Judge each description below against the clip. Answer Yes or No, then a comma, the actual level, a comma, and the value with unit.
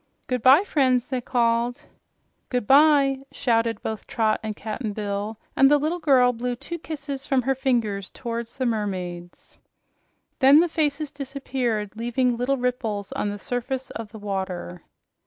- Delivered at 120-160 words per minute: Yes, average, 145 wpm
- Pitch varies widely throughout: No, average, 3.9 semitones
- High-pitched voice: Yes, high, 245 Hz